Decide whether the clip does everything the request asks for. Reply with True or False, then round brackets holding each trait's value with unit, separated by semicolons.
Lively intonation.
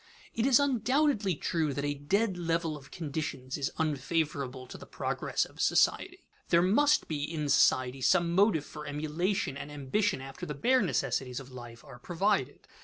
True (5.9 semitones)